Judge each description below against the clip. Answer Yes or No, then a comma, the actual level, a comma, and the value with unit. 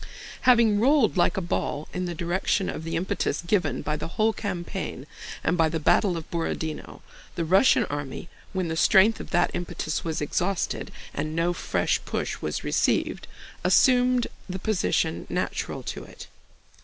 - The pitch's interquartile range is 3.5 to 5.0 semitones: Yes, average, 4.0 semitones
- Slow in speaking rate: No, average, 155 wpm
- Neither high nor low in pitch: Yes, medium, 175 Hz